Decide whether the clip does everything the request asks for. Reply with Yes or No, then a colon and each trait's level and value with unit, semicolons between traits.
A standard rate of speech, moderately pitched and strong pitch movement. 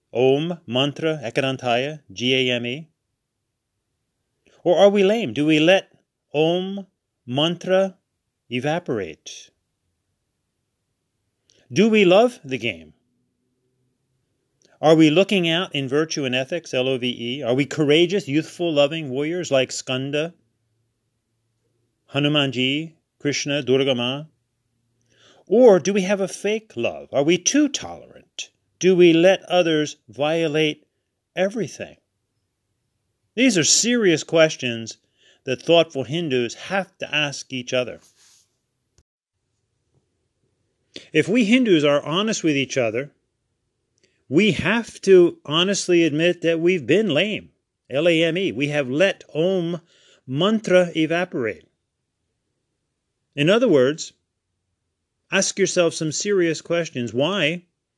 No: slow, 115 wpm; medium, 145 Hz; wide, 6.2 semitones